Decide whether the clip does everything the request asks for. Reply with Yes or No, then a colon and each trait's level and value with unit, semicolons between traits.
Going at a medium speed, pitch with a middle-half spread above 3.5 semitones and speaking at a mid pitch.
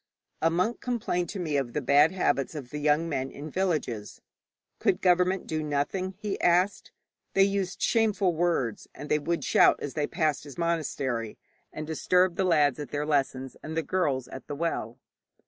Yes: average, 180 wpm; average, 4.1 semitones; medium, 155 Hz